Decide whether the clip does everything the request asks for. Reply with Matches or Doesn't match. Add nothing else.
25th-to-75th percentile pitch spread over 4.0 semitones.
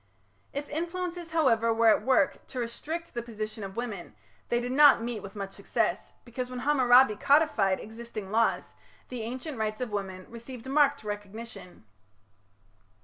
Matches